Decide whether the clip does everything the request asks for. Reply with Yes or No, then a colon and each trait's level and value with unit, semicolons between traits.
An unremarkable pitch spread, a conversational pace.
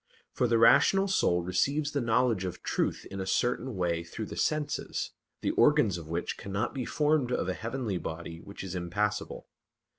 No: wide, 6.2 semitones; average, 180 wpm